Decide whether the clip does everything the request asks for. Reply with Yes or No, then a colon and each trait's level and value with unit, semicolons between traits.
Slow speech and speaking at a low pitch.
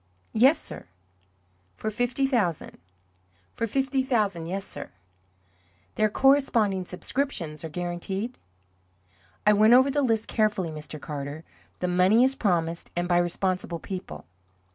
No: slow, 125 wpm; high, 200 Hz